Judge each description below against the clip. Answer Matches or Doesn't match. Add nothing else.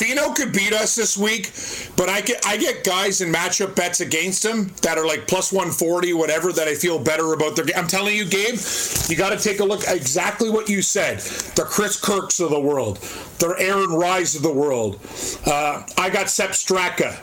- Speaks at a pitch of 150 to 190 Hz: Matches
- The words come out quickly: Matches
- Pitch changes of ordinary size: Matches